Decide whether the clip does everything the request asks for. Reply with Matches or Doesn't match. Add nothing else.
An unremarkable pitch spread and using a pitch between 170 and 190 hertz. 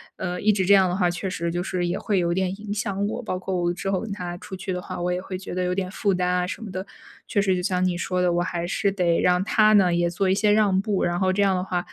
Doesn't match